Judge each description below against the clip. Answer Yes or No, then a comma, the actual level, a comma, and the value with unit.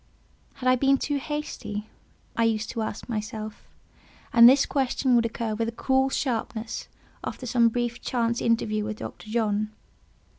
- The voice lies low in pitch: No, high, 230 Hz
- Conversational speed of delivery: Yes, average, 155 wpm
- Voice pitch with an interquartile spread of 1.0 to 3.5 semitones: Yes, average, 2.7 semitones